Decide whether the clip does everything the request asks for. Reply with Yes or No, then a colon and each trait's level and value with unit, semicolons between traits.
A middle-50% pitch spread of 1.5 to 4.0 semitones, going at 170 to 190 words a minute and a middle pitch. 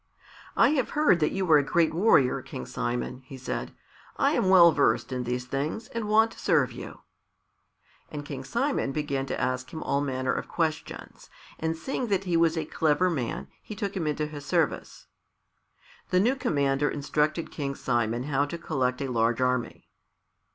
No: average, 4.9 semitones; average, 180 wpm; medium, 150 Hz